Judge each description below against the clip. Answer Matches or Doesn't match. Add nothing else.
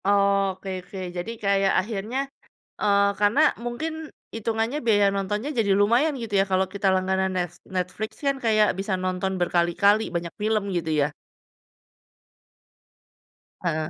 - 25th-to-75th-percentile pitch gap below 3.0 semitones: Matches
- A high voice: Matches